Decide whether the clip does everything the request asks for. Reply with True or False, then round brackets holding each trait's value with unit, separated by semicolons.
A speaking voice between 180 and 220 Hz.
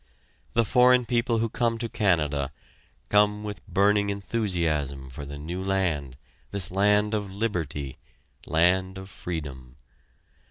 False (95 Hz)